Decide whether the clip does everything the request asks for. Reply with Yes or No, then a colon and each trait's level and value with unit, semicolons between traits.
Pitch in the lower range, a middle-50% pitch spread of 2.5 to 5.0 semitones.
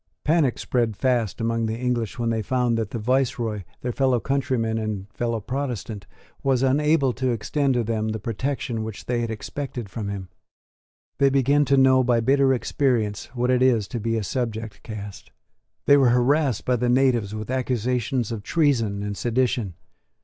Yes: low, 120 Hz; average, 2.9 semitones